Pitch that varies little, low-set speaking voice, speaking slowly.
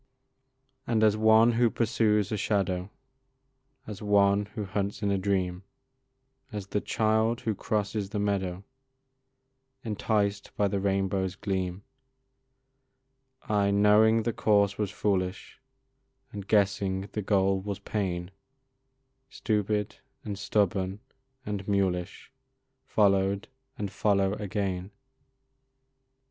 Yes: narrow, 1.6 semitones; low, 100 Hz; slow, 105 wpm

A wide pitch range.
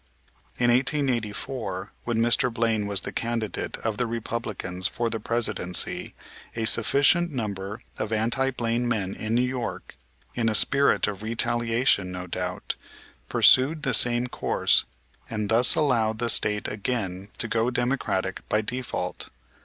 No: average, 2.8 semitones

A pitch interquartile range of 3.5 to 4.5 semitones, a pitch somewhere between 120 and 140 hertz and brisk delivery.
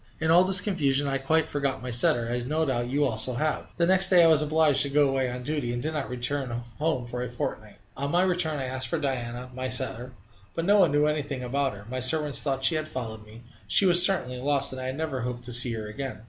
Yes: average, 3.9 semitones; low, 135 Hz; fast, 250 wpm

